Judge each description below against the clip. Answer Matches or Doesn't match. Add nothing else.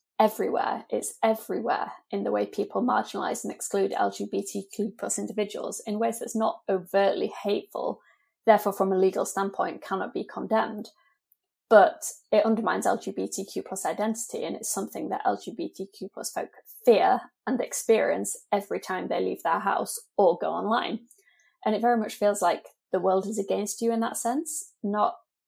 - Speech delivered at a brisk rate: Doesn't match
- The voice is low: Doesn't match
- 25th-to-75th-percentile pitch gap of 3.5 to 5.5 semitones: Doesn't match